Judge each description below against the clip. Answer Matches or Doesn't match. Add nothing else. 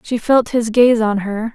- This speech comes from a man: Doesn't match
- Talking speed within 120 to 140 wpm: Doesn't match